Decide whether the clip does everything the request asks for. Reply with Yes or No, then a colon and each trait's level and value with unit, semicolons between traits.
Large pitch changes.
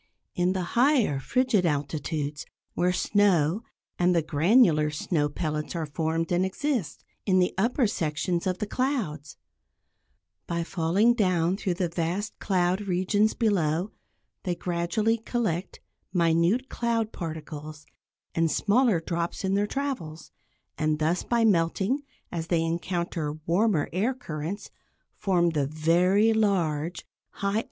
No: average, 4.2 semitones